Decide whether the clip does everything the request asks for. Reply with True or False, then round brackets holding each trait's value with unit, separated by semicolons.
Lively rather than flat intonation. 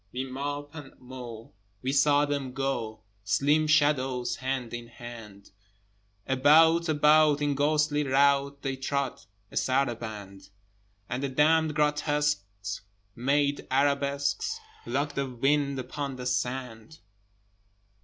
False (2.8 semitones)